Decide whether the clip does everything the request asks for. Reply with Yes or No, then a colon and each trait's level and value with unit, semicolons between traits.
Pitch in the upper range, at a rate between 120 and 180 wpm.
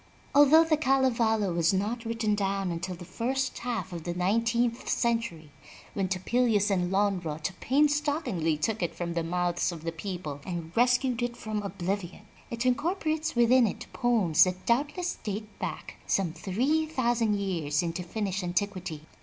Yes: high, 205 Hz; average, 155 wpm